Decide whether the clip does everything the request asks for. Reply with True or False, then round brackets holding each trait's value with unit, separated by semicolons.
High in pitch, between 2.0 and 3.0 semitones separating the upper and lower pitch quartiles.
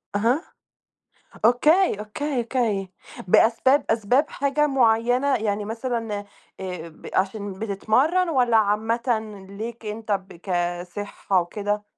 False (220 Hz; 3.6 semitones)